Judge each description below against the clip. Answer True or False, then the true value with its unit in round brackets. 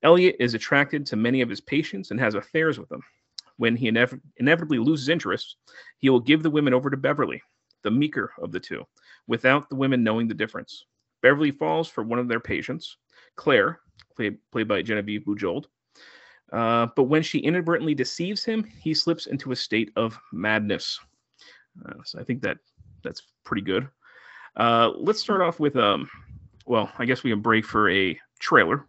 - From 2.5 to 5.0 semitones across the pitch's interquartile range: False (5.6 semitones)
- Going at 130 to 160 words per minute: False (185 wpm)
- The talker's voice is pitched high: False (125 Hz)